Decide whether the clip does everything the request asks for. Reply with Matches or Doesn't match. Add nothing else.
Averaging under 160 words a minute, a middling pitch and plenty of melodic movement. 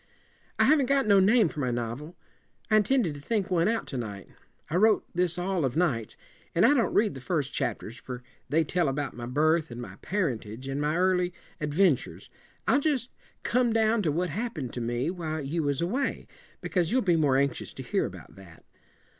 Doesn't match